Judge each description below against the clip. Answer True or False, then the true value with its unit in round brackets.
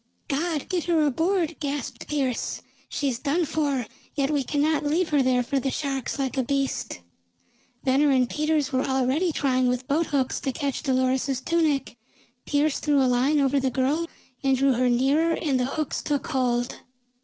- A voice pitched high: True (275 Hz)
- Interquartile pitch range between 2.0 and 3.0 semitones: True (2.7 semitones)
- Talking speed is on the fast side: False (175 wpm)